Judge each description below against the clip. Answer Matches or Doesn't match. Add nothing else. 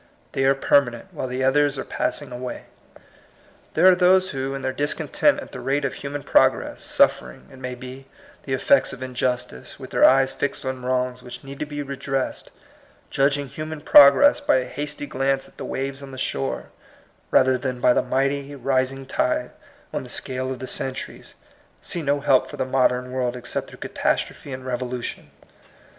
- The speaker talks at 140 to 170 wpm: Doesn't match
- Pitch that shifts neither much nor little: Doesn't match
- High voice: Doesn't match